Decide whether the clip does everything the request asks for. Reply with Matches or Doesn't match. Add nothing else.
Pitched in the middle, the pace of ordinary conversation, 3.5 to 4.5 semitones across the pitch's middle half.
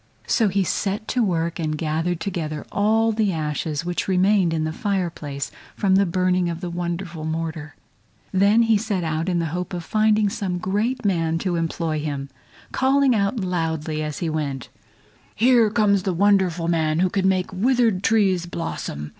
Matches